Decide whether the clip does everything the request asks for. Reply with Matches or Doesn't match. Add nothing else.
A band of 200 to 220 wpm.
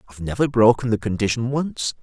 Matches